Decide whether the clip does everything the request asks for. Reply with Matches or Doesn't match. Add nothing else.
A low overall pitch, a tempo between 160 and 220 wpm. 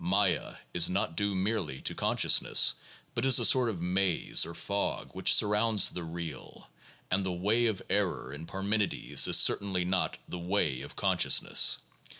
Matches